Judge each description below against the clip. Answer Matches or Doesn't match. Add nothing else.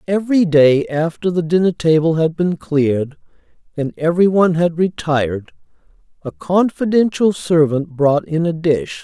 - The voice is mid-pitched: Matches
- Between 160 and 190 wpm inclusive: Doesn't match